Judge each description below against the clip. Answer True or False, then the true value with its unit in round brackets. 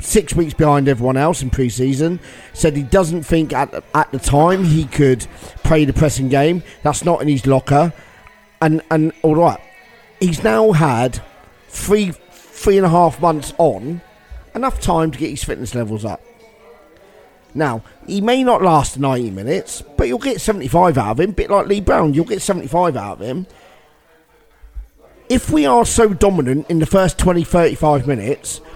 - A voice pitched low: False (160 Hz)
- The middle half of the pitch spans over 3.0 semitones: True (5.0 semitones)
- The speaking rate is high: False (175 wpm)